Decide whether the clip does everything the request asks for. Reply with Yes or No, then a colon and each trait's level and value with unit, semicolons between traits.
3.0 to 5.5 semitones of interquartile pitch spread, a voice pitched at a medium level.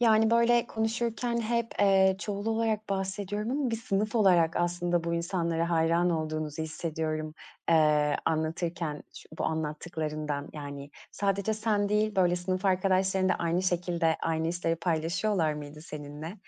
Yes: average, 4.4 semitones; medium, 175 Hz